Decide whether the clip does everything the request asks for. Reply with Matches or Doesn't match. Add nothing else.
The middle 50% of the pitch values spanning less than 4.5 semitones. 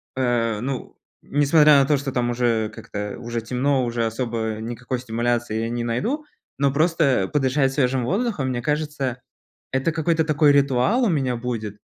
Matches